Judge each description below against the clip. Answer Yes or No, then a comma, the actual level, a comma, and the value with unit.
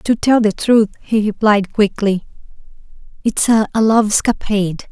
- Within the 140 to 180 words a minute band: Yes, average, 145 wpm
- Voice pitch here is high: Yes, high, 215 Hz